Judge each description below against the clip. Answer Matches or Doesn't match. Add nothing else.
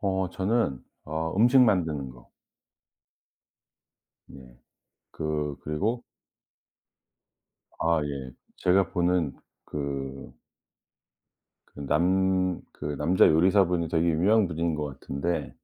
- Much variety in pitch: Doesn't match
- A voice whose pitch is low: Matches